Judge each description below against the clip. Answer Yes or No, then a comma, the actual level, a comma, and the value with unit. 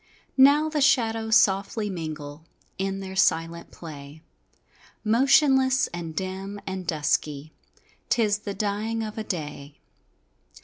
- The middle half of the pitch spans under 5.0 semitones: No, wide, 5.5 semitones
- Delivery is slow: Yes, slow, 115 wpm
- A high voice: Yes, high, 195 Hz